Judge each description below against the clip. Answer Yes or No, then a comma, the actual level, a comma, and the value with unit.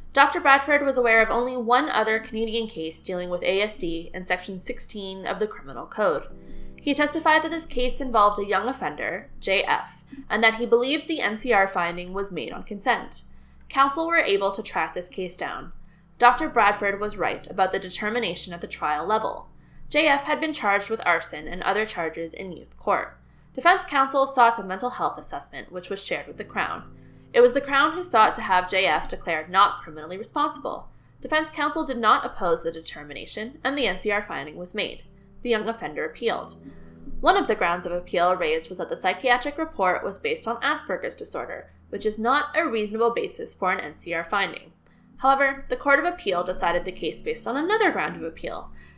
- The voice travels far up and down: Yes, wide, 6.8 semitones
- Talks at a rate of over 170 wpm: Yes, average, 190 wpm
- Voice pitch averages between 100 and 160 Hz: No, high, 225 Hz